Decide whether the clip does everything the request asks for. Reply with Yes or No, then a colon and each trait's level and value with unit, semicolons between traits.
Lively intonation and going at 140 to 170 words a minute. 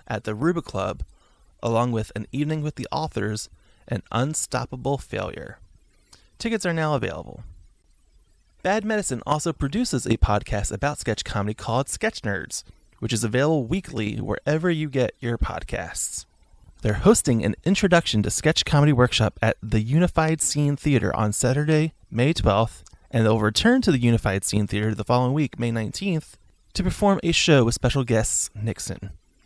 Yes: wide, 6.3 semitones; average, 155 wpm